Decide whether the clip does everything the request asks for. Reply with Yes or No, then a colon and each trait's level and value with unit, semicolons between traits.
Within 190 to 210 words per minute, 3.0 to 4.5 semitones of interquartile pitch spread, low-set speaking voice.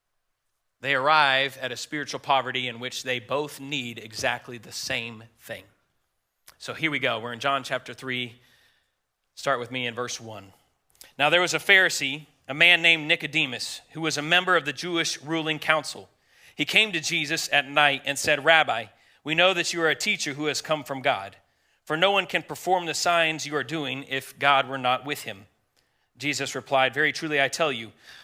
No: average, 195 wpm; average, 3.9 semitones; medium, 145 Hz